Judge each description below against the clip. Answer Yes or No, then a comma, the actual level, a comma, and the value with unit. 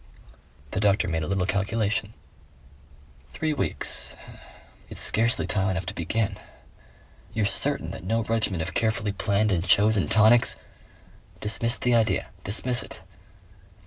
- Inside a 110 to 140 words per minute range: Yes, slow, 135 wpm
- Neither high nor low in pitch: No, low, 105 Hz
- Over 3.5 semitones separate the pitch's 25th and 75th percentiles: No, average, 2.7 semitones